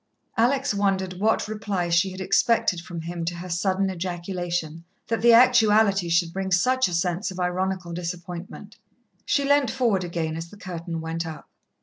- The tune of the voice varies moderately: Yes, average, 3.3 semitones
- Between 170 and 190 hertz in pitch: Yes, medium, 185 Hz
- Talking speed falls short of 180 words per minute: Yes, average, 165 wpm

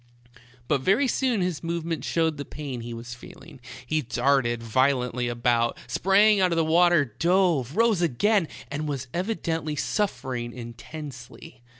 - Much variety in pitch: Yes, wide, 6.0 semitones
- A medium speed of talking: Yes, average, 155 wpm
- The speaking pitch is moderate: Yes, medium, 150 Hz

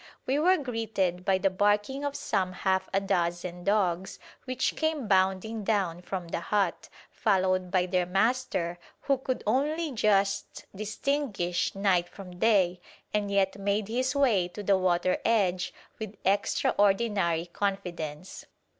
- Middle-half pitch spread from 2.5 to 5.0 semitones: Yes, average, 3.3 semitones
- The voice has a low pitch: No, high, 195 Hz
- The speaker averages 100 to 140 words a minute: Yes, slow, 135 wpm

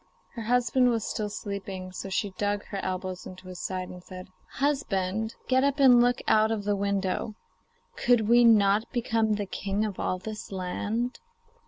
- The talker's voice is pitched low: No, high, 205 Hz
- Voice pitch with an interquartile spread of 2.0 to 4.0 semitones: Yes, average, 3.6 semitones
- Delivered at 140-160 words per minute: No, average, 175 wpm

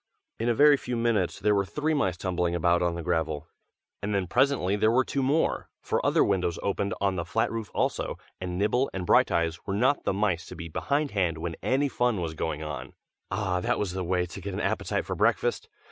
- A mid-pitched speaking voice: No, very low, 95 Hz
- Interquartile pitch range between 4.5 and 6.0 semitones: Yes, average, 5.0 semitones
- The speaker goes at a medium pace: No, fast, 220 wpm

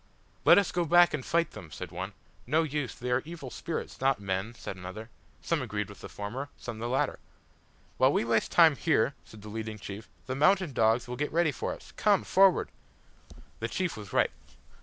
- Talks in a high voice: No, low, 125 Hz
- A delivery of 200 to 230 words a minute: Yes, fast, 205 wpm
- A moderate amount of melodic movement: No, wide, 7.1 semitones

